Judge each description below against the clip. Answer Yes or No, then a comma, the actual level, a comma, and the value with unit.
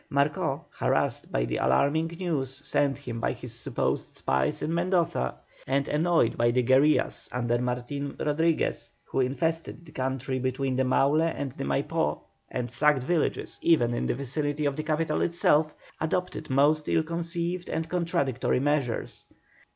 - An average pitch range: Yes, average, 3.9 semitones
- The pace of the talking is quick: No, average, 150 wpm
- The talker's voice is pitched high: No, medium, 145 Hz